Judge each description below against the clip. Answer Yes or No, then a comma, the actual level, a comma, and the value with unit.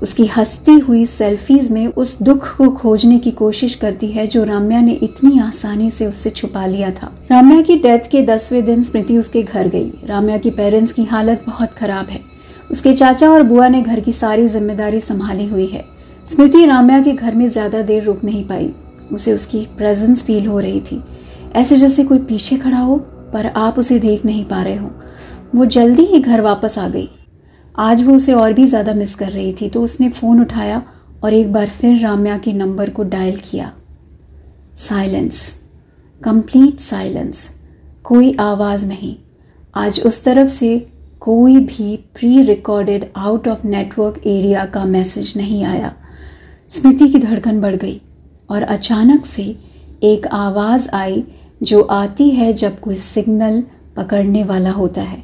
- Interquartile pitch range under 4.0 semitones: Yes, average, 3.0 semitones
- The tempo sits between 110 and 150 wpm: No, average, 175 wpm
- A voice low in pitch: No, high, 220 Hz